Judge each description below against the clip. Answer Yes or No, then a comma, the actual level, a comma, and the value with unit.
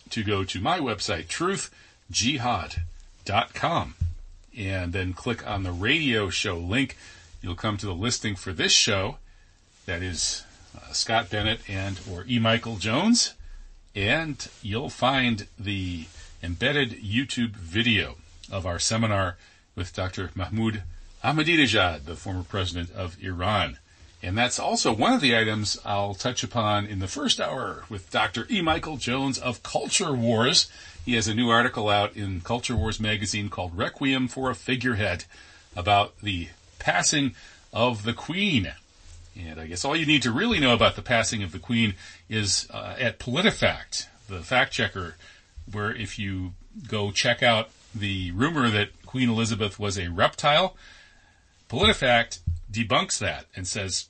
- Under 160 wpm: Yes, average, 150 wpm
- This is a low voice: Yes, low, 105 Hz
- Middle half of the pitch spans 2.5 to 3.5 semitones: No, average, 4.6 semitones